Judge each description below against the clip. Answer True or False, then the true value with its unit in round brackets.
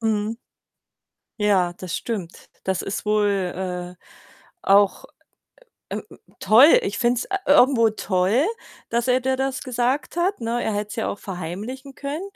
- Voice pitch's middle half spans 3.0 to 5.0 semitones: True (4.4 semitones)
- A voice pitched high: True (230 Hz)